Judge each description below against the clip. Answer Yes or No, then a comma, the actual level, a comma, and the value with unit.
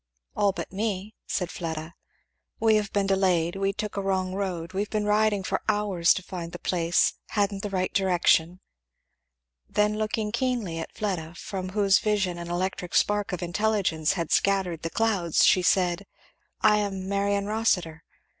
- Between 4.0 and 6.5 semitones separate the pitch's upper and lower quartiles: No, average, 2.9 semitones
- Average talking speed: Yes, average, 165 wpm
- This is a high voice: Yes, high, 195 Hz